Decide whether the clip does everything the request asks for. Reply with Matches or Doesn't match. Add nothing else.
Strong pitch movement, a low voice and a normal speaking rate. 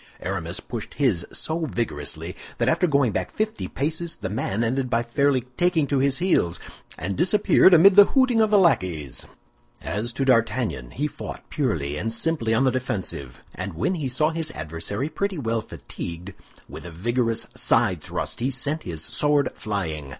Matches